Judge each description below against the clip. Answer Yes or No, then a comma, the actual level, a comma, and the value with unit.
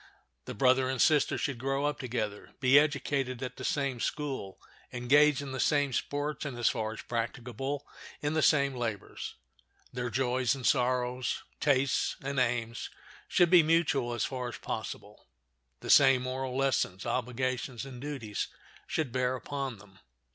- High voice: No, low, 130 Hz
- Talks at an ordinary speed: Yes, average, 155 wpm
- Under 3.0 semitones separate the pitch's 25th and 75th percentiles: Yes, narrow, 2.4 semitones